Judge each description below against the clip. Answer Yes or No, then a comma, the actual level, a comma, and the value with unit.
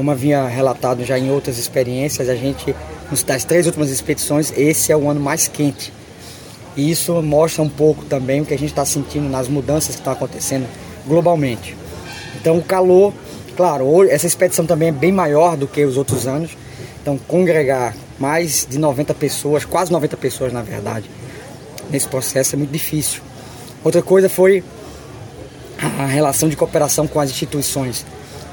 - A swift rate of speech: No, average, 165 wpm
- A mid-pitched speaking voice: Yes, medium, 145 Hz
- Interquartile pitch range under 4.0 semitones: Yes, average, 3.2 semitones